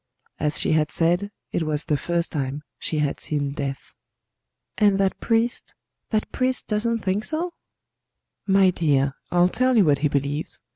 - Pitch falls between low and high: Yes, medium, 170 Hz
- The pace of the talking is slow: No, average, 160 wpm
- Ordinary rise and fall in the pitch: No, wide, 6.2 semitones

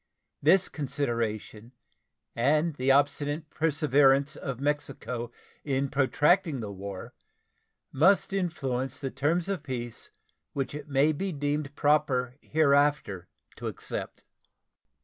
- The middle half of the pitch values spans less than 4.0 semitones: Yes, average, 2.9 semitones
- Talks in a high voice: No, medium, 140 Hz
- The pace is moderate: No, slow, 110 wpm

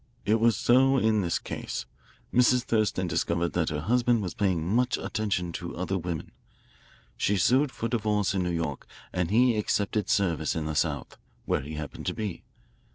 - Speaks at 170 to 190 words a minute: Yes, average, 175 wpm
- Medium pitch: No, low, 100 Hz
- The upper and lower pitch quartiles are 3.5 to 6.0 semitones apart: Yes, average, 5.0 semitones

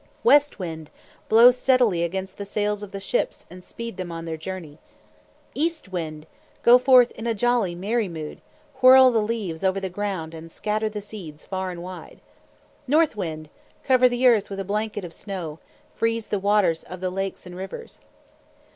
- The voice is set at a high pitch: Yes, high, 195 Hz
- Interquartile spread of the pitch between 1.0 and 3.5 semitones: No, average, 4.7 semitones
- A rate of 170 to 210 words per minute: Yes, average, 180 wpm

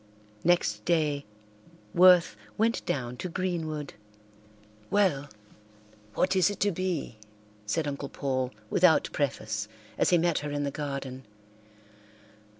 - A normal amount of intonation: Yes, average, 4.6 semitones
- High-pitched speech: No, medium, 150 Hz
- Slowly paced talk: Yes, slow, 120 wpm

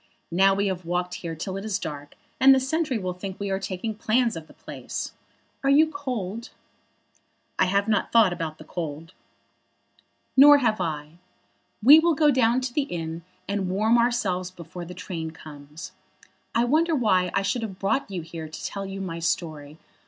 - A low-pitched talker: No, high, 195 Hz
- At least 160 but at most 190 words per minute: Yes, average, 185 wpm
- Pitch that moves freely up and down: Yes, wide, 5.8 semitones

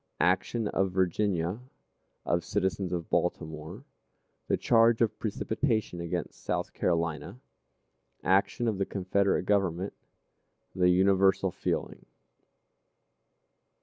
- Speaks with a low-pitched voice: Yes, very low, 95 Hz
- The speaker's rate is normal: No, slow, 95 wpm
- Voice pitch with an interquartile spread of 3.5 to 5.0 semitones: No, average, 2.9 semitones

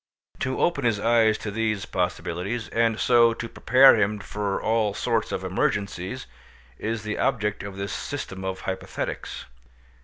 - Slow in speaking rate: No, average, 150 wpm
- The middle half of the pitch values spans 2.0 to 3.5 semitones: Yes, average, 2.8 semitones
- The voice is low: Yes, low, 105 Hz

